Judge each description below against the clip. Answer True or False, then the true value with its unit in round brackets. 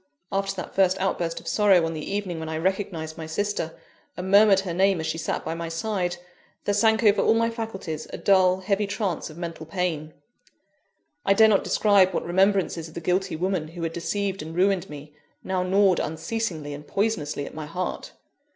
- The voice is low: False (185 Hz)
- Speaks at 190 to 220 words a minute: True (195 wpm)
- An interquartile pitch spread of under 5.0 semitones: True (3.4 semitones)